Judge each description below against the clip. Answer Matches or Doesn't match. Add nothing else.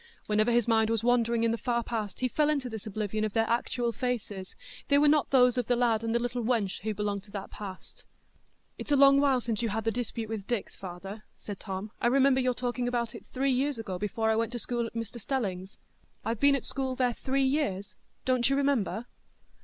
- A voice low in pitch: Doesn't match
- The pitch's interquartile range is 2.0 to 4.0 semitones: Matches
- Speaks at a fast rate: Matches